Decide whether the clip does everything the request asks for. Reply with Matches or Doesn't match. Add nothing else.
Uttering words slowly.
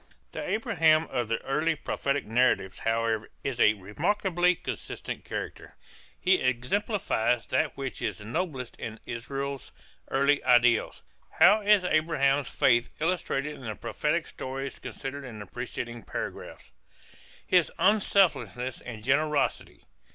Matches